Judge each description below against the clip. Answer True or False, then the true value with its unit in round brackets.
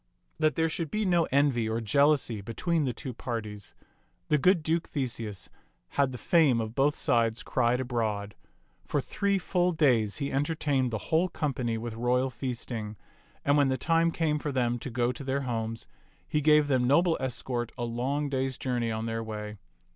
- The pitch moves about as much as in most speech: True (4.5 semitones)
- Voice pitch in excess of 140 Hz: False (130 Hz)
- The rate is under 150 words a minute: False (185 wpm)